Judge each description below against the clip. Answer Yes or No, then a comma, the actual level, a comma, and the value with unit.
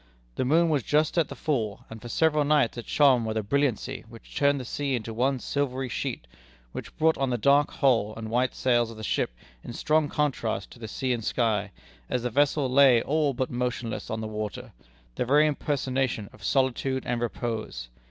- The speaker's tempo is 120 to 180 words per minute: No, average, 200 wpm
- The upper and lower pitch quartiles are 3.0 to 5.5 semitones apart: Yes, average, 3.8 semitones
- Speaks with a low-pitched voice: Yes, low, 125 Hz